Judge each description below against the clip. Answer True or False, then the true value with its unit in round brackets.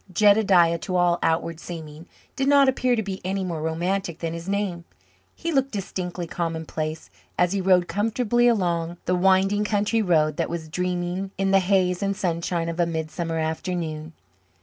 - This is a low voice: False (180 Hz)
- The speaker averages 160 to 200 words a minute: True (170 wpm)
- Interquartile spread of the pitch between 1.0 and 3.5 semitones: True (3.0 semitones)